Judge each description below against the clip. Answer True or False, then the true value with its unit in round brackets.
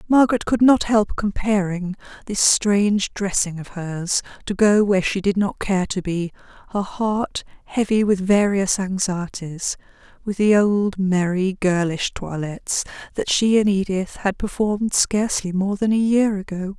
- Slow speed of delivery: False (145 wpm)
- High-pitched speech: True (195 Hz)